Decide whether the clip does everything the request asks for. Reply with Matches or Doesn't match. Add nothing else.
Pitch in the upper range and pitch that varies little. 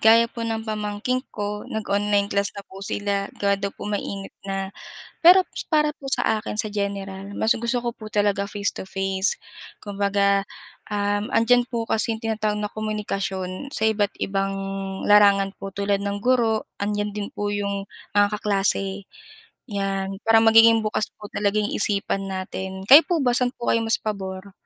Matches